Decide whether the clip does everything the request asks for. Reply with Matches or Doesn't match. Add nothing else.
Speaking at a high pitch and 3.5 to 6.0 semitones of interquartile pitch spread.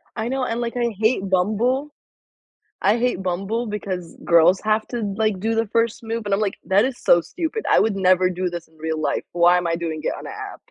Matches